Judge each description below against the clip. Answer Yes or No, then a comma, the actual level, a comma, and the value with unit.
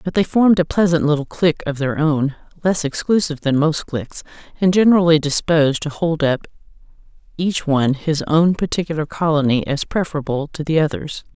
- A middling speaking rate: Yes, average, 170 wpm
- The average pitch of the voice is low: No, medium, 155 Hz